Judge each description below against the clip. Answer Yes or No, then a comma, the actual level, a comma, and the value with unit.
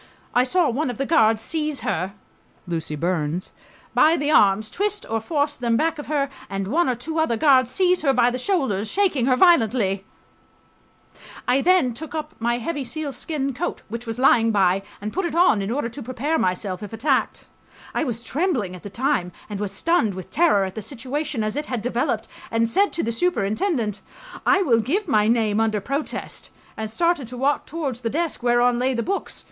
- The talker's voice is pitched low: No, very high, 250 Hz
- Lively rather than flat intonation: Yes, wide, 5.9 semitones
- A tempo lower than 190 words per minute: No, average, 200 wpm